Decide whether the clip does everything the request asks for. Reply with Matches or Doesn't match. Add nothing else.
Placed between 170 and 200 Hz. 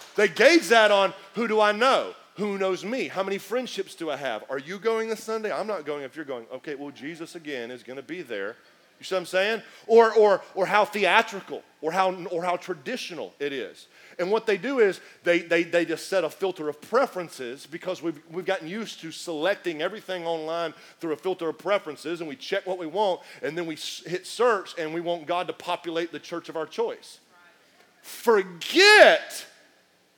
Matches